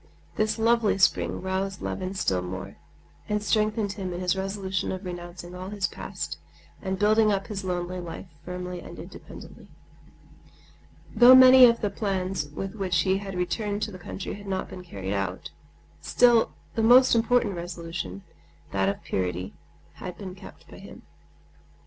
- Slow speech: No, average, 155 wpm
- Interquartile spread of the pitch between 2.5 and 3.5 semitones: Yes, average, 3.1 semitones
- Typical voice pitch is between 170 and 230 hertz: Yes, high, 190 Hz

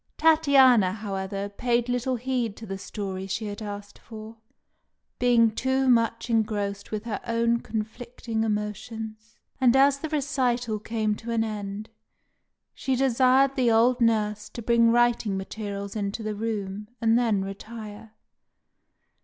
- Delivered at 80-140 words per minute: Yes, slow, 135 wpm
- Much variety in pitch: No, narrow, 2.6 semitones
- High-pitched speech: Yes, high, 225 Hz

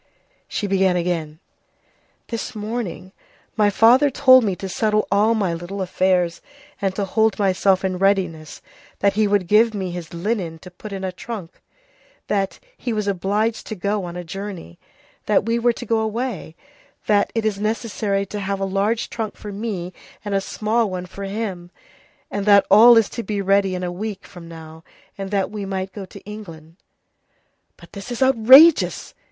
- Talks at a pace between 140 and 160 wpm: No, average, 180 wpm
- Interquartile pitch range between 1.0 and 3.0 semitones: Yes, average, 2.7 semitones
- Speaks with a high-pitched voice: Yes, high, 200 Hz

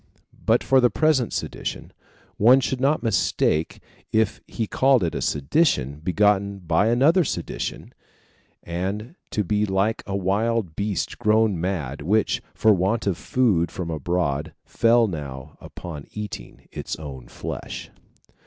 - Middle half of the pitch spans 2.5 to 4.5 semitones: No, wide, 5.4 semitones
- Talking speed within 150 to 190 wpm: No, slow, 135 wpm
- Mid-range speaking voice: No, low, 100 Hz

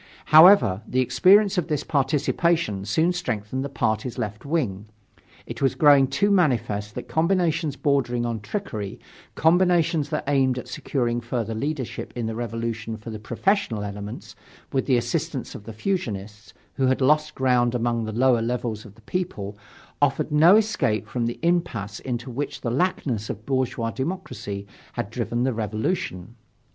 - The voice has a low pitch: Yes, low, 125 Hz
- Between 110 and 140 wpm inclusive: No, average, 155 wpm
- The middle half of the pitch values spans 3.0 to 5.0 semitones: No, wide, 5.6 semitones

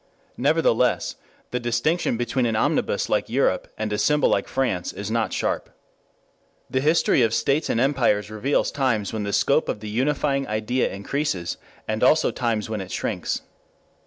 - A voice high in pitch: No, low, 120 Hz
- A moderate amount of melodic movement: Yes, average, 4.3 semitones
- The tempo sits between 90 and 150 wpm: No, average, 160 wpm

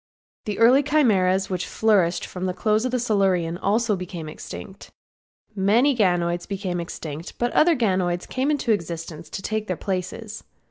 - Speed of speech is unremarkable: Yes, average, 145 wpm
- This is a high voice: Yes, high, 195 Hz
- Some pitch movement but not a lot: Yes, average, 4.1 semitones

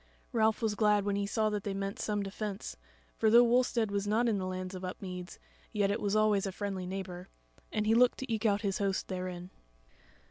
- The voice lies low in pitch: No, high, 205 Hz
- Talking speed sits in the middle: No, fast, 215 wpm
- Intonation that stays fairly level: Yes, narrow, 2.1 semitones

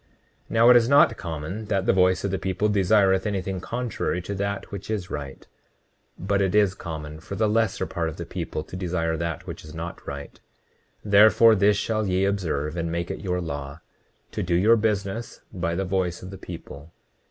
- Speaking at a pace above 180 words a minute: Yes, average, 200 wpm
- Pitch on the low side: Yes, very low, 95 Hz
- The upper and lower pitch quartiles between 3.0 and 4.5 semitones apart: Yes, average, 3.5 semitones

